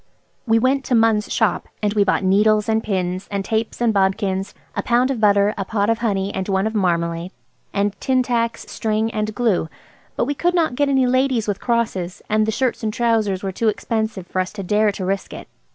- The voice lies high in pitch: Yes, high, 215 Hz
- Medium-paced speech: No, fast, 215 wpm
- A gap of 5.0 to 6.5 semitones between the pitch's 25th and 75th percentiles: No, average, 3.0 semitones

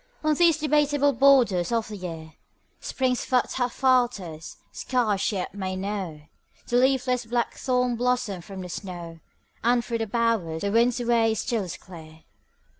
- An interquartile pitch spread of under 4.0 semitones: No, average, 5.0 semitones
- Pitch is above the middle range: Yes, high, 230 Hz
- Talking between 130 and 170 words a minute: Yes, average, 155 wpm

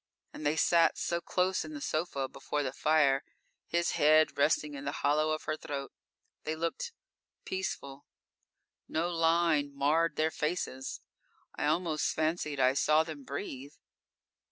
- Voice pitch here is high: No, medium, 155 Hz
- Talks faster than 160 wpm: No, average, 145 wpm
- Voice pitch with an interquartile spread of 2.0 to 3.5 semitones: Yes, average, 2.7 semitones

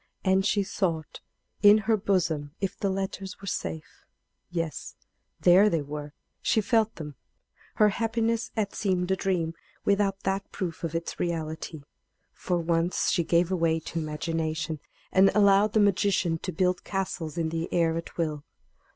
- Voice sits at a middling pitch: Yes, medium, 180 Hz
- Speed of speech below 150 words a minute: No, average, 155 wpm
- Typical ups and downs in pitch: Yes, average, 3.3 semitones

